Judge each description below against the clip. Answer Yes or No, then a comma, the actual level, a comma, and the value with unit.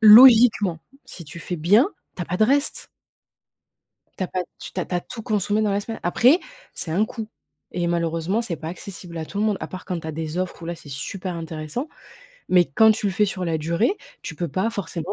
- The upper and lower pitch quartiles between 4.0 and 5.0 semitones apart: Yes, average, 4.3 semitones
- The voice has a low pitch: No, medium, 185 Hz